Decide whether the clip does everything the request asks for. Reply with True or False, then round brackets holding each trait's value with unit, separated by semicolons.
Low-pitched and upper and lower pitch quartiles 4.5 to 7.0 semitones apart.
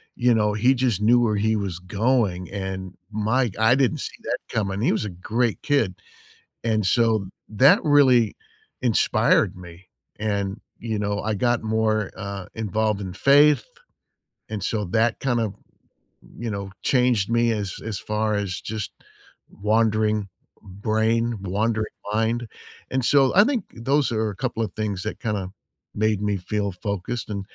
False (110 Hz; 2.7 semitones)